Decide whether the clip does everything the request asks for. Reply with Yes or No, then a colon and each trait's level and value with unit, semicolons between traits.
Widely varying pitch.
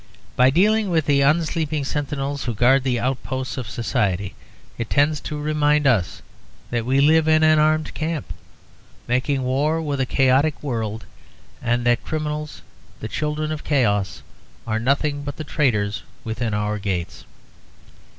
No: average, 4.2 semitones